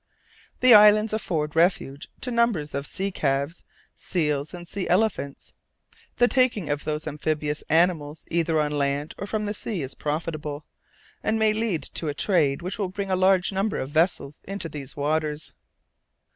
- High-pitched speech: No, medium, 165 Hz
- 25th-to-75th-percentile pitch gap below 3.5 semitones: No, average, 5.2 semitones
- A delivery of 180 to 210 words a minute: No, average, 165 wpm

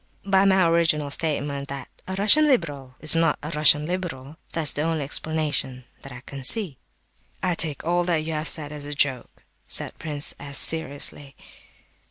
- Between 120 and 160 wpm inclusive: No, average, 175 wpm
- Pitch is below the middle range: No, medium, 150 Hz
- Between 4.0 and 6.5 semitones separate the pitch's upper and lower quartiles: No, average, 2.9 semitones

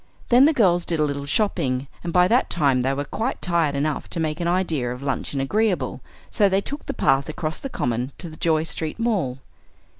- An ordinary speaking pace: No, fast, 215 wpm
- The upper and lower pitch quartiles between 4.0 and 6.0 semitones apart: Yes, average, 5.1 semitones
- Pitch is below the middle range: No, medium, 160 Hz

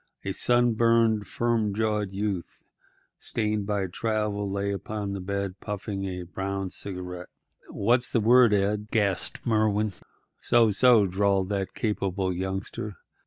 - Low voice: Yes, low, 100 Hz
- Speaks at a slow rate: Yes, slow, 130 wpm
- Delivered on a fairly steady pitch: Yes, narrow, 2.0 semitones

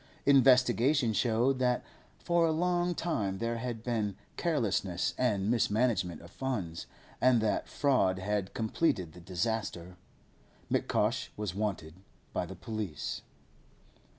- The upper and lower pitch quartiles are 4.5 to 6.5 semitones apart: Yes, average, 5.1 semitones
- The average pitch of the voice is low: Yes, low, 110 Hz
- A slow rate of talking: Yes, slow, 120 wpm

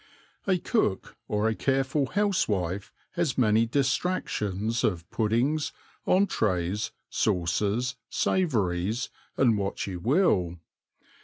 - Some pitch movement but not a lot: No, wide, 6.0 semitones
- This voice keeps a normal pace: No, slow, 95 wpm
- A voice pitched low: Yes, low, 115 Hz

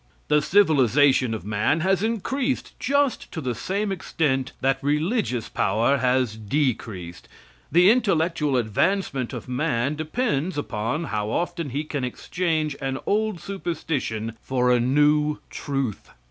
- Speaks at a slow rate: Yes, slow, 130 wpm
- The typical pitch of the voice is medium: Yes, medium, 145 Hz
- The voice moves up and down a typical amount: No, wide, 5.7 semitones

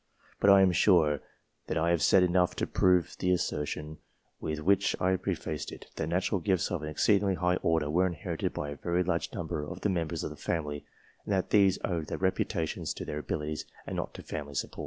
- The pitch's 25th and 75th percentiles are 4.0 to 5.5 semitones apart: No, average, 3.4 semitones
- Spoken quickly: Yes, fast, 210 wpm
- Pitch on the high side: No, very low, 85 Hz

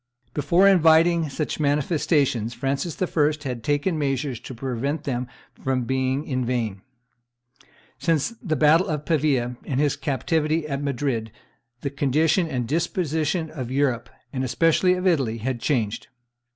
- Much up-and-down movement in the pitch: No, average, 3.7 semitones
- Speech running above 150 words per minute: No, average, 140 wpm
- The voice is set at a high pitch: No, medium, 145 Hz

